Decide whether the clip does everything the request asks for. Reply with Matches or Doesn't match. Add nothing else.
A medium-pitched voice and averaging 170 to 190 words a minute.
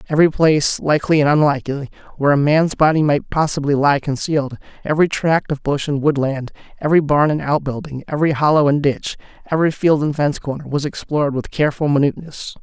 Matches